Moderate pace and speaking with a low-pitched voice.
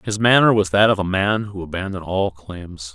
No: fast, 225 wpm; very low, 95 Hz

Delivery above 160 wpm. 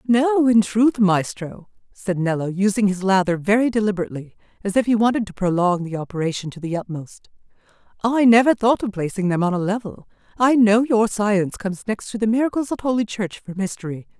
Yes: average, 190 wpm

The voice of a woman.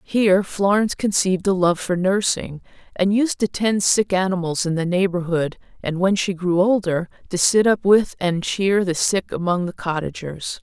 Yes: female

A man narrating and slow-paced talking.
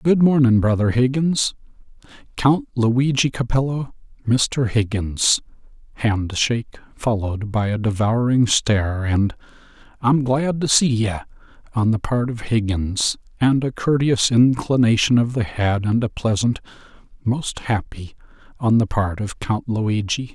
Yes: male; slow, 125 wpm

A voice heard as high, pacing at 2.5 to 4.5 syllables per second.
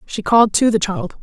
No: high, 215 Hz; 5.6 syllables/s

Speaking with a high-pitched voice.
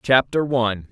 No: low, 120 Hz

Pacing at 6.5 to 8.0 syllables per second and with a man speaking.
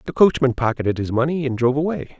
Yes: 6.8 syllables/s; male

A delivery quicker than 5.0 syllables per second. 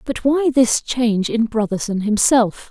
No: 4.2 syllables/s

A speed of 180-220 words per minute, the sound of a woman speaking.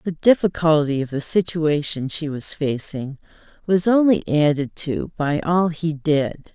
No: average, 145 wpm; female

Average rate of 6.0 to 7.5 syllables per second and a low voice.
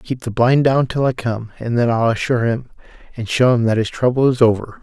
No: 5.6 syllables/s; low, 120 Hz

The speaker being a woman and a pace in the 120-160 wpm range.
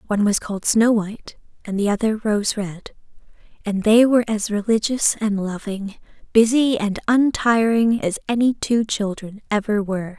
Yes: female; average, 155 wpm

